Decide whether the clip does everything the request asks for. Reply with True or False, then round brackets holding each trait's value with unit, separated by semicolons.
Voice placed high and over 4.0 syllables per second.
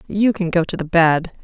False (175 Hz; 5.1 syllables/s)